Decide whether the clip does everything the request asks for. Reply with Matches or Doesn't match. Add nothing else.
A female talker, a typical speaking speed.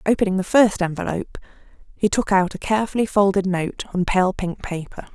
Matches